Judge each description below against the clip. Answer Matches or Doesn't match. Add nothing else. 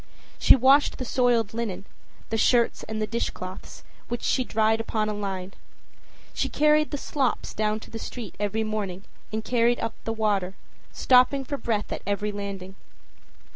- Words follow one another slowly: Doesn't match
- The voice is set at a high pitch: Matches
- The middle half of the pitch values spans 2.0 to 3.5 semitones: Matches